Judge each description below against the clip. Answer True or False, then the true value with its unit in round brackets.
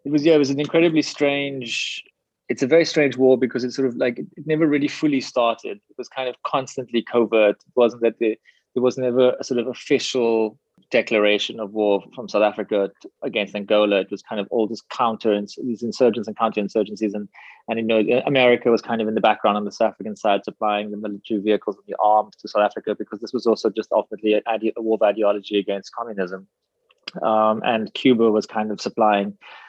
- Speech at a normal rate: False (210 wpm)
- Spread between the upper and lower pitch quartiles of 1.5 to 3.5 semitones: True (3.1 semitones)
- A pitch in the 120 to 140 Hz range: False (110 Hz)